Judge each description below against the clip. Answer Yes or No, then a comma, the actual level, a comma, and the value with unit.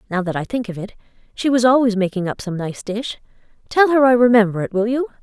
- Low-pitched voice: No, high, 225 Hz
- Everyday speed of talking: No, fast, 240 wpm